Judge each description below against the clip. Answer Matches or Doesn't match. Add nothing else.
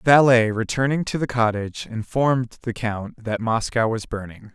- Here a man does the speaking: Matches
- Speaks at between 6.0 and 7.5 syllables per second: Doesn't match